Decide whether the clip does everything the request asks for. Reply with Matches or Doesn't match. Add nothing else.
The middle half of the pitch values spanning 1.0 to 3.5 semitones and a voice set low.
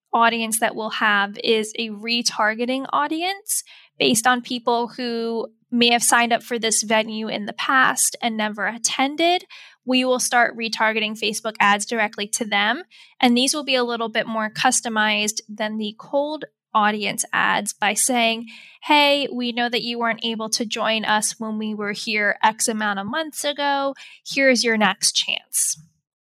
Doesn't match